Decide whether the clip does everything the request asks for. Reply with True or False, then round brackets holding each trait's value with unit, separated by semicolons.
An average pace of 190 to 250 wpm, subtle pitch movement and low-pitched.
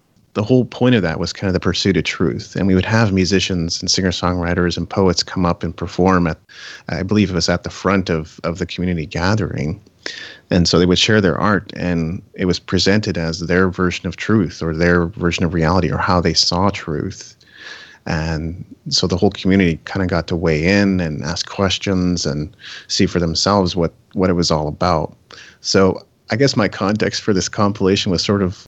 True (205 wpm; 2.3 semitones; 90 Hz)